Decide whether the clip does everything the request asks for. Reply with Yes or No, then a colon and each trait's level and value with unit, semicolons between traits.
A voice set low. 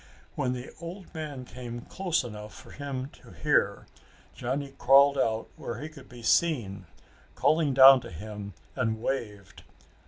Yes: low, 130 Hz